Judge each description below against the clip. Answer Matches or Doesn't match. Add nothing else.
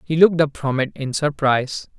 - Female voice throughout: Doesn't match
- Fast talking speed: Matches